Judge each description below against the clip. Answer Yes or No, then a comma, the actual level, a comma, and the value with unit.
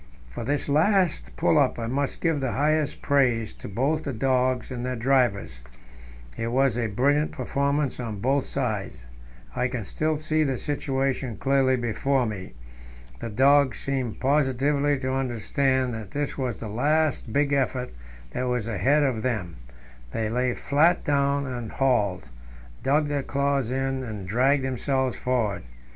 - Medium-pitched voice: No, low, 130 Hz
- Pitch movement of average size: Yes, average, 3.1 semitones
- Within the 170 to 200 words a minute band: No, average, 155 wpm